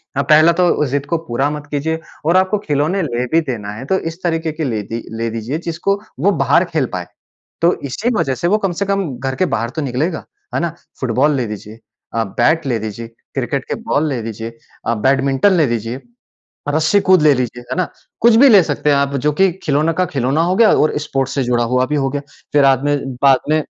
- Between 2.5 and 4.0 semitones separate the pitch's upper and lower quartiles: No, average, 4.7 semitones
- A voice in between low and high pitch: Yes, medium, 145 Hz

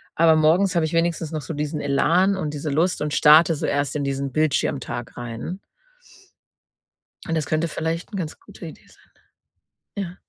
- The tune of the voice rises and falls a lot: No, average, 2.7 semitones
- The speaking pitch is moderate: Yes, medium, 155 Hz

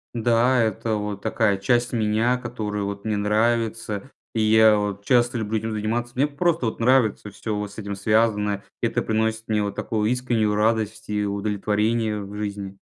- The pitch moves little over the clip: Yes, narrow, 2.0 semitones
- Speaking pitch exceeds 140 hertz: No, low, 110 Hz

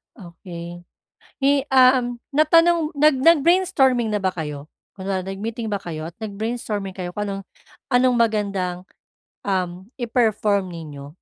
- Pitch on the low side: No, high, 210 Hz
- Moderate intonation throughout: No, wide, 5.7 semitones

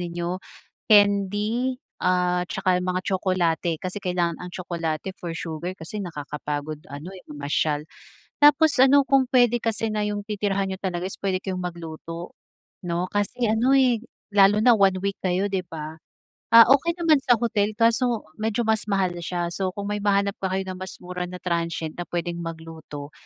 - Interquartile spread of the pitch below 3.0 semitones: No, average, 3.6 semitones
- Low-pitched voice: No, medium, 185 Hz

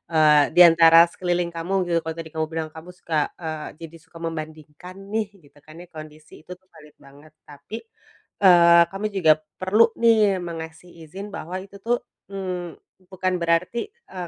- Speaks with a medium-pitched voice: Yes, medium, 170 Hz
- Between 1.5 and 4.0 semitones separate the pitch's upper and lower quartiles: Yes, average, 2.9 semitones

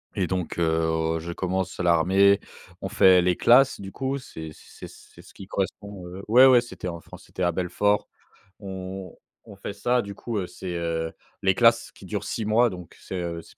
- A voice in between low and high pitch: No, very low, 95 Hz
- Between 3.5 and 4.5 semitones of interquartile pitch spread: No, average, 2.9 semitones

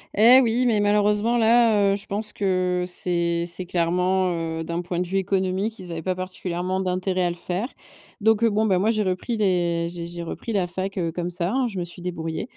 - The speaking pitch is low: No, medium, 185 Hz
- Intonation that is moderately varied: Yes, average, 3.0 semitones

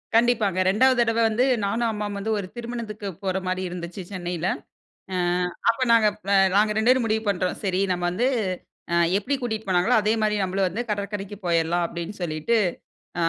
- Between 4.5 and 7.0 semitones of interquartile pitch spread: No, average, 3.6 semitones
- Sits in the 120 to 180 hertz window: No, high, 205 Hz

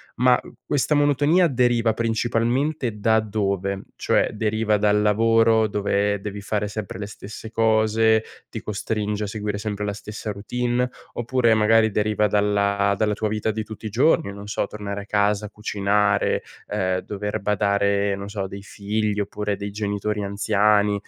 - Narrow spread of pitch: Yes, narrow, 1.6 semitones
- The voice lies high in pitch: No, low, 105 Hz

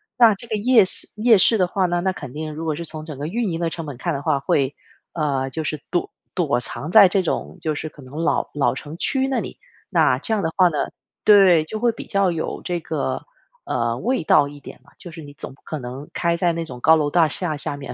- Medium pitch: Yes, medium, 165 Hz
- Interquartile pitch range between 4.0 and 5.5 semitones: Yes, average, 4.3 semitones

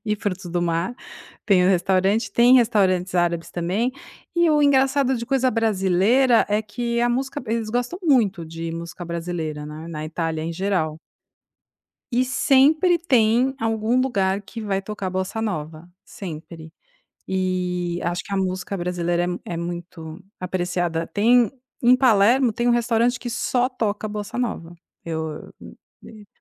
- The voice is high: Yes, high, 200 Hz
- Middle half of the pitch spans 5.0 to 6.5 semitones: Yes, wide, 5.6 semitones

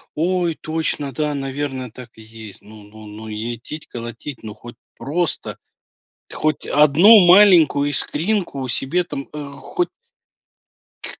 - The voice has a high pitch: No, medium, 140 Hz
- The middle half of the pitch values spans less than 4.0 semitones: No, wide, 5.4 semitones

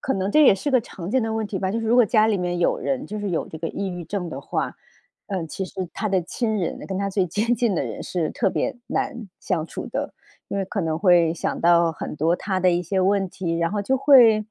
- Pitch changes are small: No, average, 3.8 semitones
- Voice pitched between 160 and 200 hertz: Yes, high, 190 Hz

